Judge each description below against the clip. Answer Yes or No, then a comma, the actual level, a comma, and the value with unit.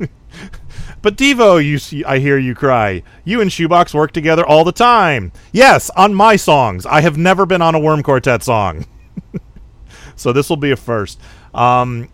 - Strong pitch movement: Yes, wide, 6.1 semitones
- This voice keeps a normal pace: Yes, average, 180 wpm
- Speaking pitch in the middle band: Yes, medium, 150 Hz